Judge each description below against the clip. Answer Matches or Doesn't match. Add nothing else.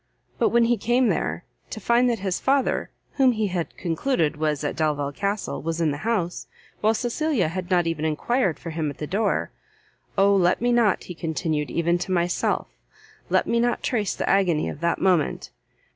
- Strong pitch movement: Matches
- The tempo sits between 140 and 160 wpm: Doesn't match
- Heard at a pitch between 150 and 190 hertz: Matches